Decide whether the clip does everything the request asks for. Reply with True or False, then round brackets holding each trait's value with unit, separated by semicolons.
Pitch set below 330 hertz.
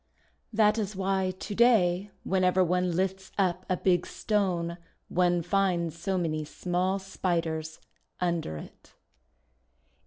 True (185 Hz)